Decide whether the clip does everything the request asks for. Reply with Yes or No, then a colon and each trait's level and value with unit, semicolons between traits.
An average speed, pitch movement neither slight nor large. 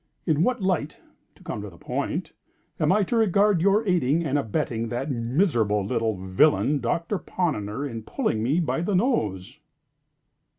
No: average, 160 wpm; wide, 8.3 semitones